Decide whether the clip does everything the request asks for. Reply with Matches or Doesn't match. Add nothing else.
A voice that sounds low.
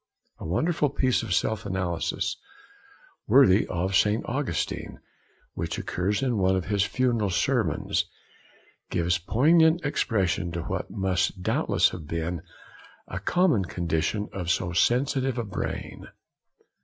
Matches